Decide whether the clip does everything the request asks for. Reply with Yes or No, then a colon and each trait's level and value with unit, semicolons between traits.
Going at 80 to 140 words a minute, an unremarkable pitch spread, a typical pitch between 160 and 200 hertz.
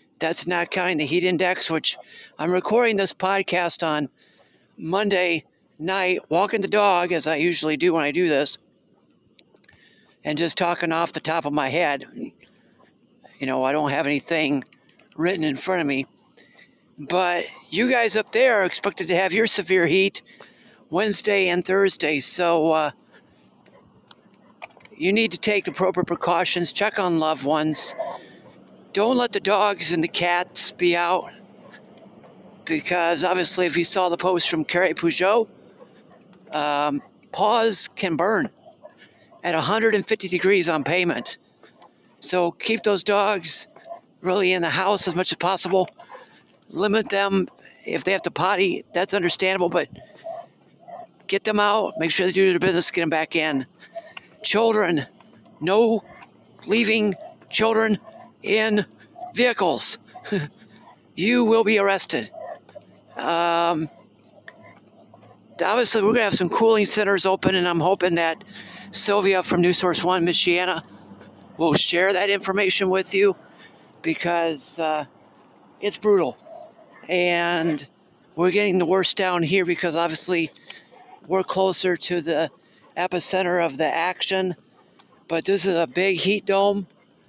Yes: slow, 135 wpm; average, 3.3 semitones; medium, 185 Hz